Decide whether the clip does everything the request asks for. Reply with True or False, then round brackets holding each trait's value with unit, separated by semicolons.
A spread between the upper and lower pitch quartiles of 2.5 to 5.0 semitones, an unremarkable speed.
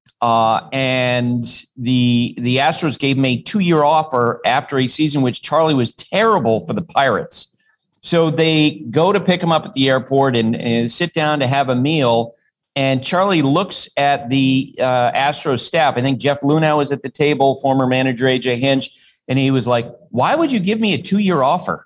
True (3.5 semitones; 190 wpm)